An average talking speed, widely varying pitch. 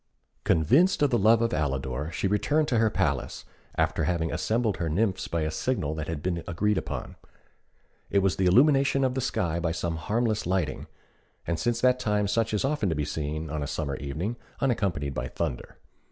Yes: average, 195 wpm; wide, 6.8 semitones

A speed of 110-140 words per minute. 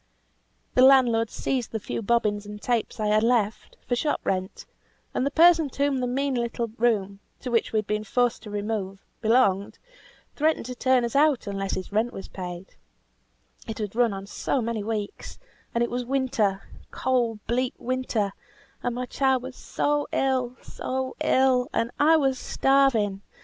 No: average, 170 wpm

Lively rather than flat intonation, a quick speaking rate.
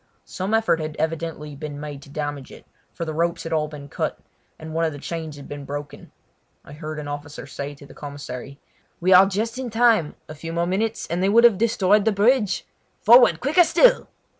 Yes: wide, 5.9 semitones; fast, 215 wpm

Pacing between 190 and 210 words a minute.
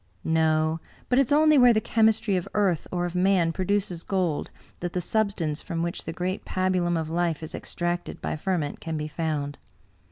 Yes: average, 195 wpm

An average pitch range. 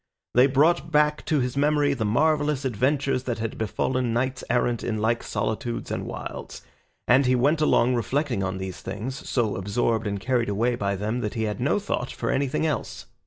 Yes: average, 4.0 semitones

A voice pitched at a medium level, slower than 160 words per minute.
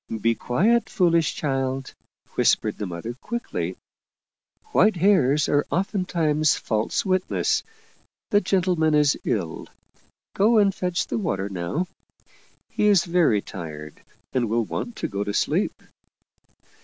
Yes: medium, 155 Hz; slow, 135 wpm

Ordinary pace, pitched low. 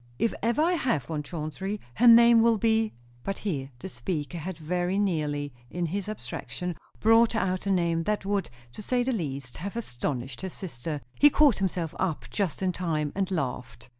No: average, 190 wpm; medium, 180 Hz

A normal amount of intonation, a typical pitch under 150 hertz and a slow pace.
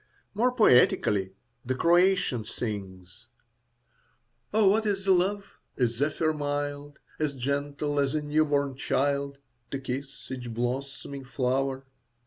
Yes: average, 3.3 semitones; medium, 140 Hz; slow, 115 wpm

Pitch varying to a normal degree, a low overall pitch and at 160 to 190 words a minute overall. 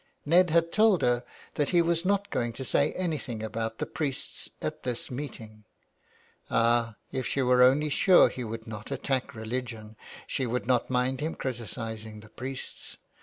Yes: average, 4.5 semitones; low, 125 Hz; average, 170 wpm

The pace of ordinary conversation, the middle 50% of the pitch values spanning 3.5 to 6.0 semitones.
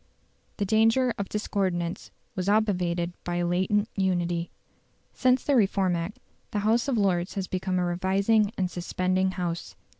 No: average, 150 wpm; average, 3.0 semitones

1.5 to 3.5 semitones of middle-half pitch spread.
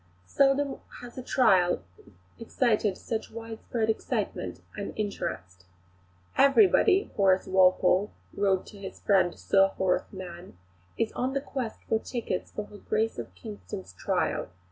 No: average, 4.3 semitones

